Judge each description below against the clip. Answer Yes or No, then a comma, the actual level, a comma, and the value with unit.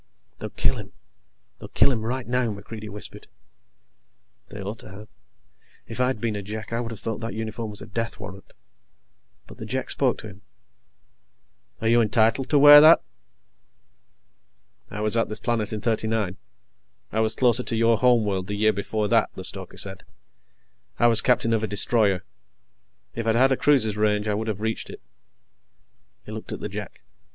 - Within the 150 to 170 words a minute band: No, average, 185 wpm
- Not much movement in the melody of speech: Yes, narrow, 1.9 semitones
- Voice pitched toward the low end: Yes, low, 110 Hz